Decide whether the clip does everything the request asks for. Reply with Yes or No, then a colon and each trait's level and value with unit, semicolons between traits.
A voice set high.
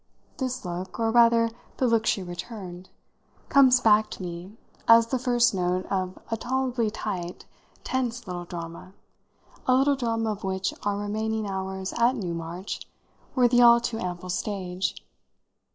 Yes: high, 215 Hz